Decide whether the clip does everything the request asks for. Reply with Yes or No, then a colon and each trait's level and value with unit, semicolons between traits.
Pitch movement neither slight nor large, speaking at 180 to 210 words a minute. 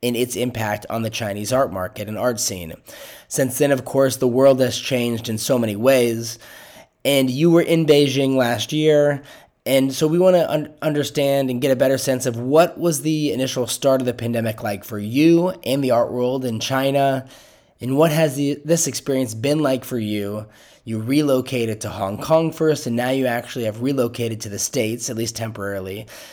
Yes: average, 3.6 semitones; average, 200 wpm